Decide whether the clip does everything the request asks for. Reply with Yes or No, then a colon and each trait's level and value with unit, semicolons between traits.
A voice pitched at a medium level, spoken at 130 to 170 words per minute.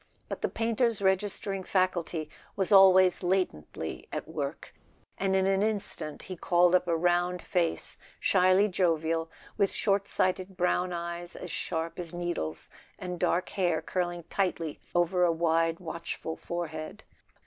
Yes: medium, 180 Hz; average, 145 wpm